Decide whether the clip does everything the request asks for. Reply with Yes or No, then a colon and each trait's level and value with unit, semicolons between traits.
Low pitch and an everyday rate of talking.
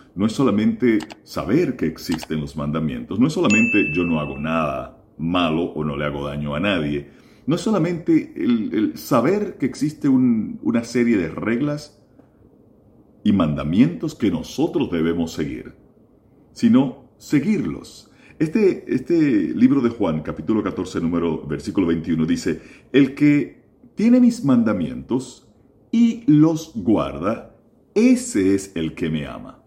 Yes: low, 125 Hz; average, 140 wpm